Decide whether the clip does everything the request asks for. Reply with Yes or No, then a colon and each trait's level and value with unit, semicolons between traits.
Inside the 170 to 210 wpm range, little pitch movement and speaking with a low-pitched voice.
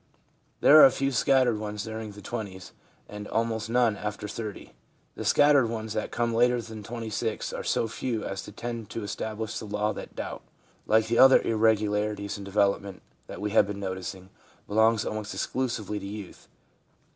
Yes: average, 175 wpm; narrow, 1.9 semitones; low, 110 Hz